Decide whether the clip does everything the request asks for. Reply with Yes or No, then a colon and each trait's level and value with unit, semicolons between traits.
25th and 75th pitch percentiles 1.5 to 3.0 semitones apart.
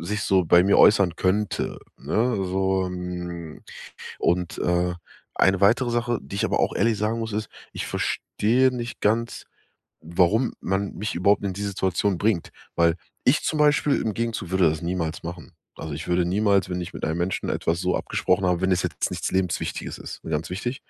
No: average, 3.4 semitones